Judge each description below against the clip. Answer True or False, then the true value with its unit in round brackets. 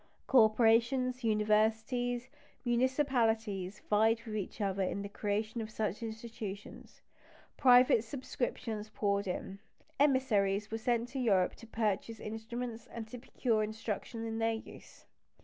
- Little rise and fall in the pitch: True (2.2 semitones)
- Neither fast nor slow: False (125 wpm)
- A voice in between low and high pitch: False (225 Hz)